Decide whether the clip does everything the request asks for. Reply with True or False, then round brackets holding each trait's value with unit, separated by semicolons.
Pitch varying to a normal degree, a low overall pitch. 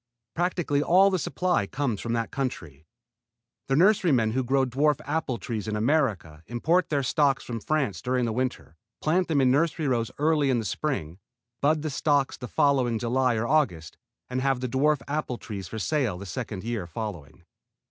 True (5.0 semitones; 130 Hz)